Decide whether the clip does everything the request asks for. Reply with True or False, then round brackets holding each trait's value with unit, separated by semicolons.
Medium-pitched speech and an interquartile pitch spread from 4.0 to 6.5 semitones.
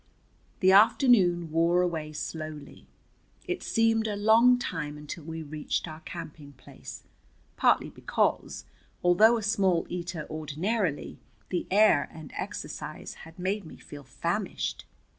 True (175 Hz; 5.2 semitones)